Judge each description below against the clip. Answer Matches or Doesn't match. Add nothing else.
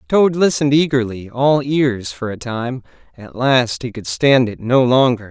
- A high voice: Doesn't match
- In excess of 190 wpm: Doesn't match